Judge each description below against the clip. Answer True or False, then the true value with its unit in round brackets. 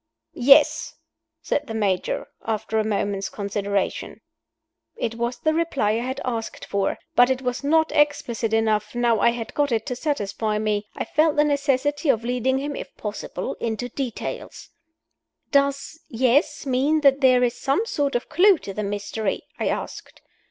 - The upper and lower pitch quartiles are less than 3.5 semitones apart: False (4.6 semitones)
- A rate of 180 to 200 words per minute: False (165 wpm)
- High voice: True (245 Hz)